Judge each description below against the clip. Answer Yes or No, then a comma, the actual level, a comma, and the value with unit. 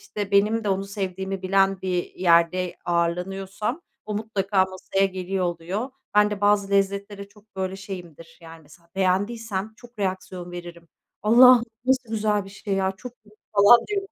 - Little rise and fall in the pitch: Yes, narrow, 2.1 semitones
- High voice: Yes, high, 195 Hz